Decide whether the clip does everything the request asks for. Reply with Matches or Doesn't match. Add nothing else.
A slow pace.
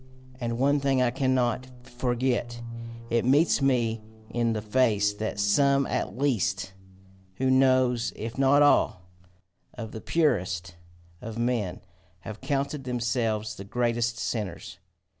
Matches